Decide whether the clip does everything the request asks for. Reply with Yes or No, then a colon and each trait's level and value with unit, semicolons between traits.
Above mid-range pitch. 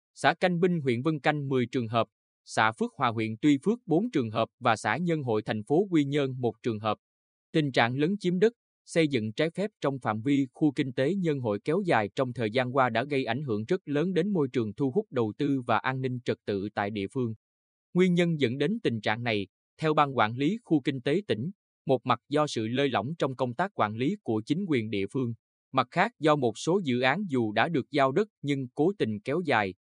No: low, 130 Hz